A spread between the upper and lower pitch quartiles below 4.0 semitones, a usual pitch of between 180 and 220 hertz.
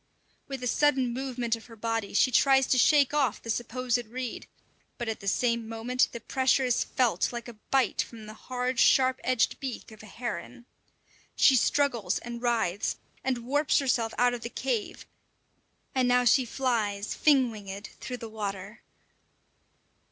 No: narrow, 2.4 semitones; high, 240 Hz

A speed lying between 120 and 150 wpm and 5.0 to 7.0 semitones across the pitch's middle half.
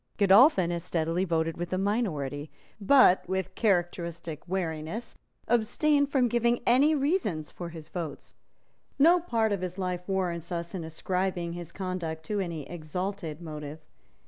No: average, 145 wpm; average, 4.2 semitones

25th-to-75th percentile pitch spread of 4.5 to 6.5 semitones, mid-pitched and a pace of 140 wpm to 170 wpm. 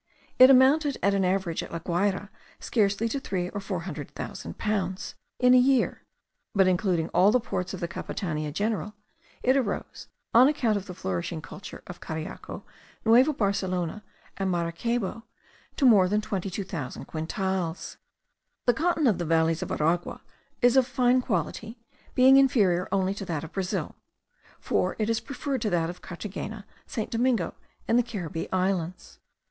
No: average, 5.0 semitones; high, 195 Hz; average, 160 wpm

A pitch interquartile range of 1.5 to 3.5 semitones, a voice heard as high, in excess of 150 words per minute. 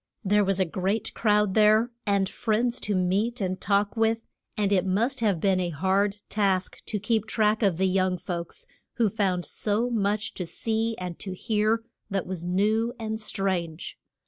Yes: average, 2.8 semitones; high, 205 Hz; average, 175 wpm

